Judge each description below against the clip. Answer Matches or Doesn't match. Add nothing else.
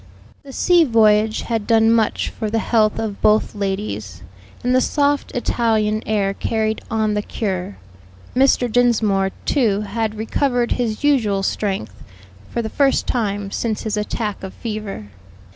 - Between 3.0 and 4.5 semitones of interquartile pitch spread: Doesn't match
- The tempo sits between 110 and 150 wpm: Matches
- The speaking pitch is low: Doesn't match